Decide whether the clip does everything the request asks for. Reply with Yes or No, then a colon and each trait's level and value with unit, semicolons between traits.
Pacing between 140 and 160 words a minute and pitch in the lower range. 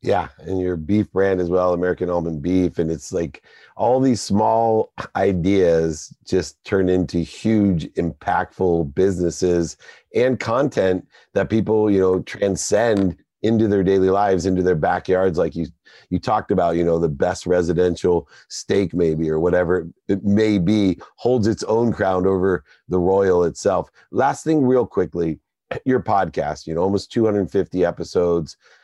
Yes: average, 150 wpm; very low, 95 Hz